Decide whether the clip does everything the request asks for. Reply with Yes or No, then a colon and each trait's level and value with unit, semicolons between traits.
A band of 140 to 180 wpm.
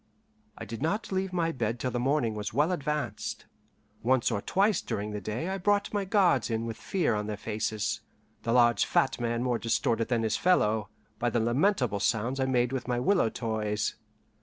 No: average, 195 wpm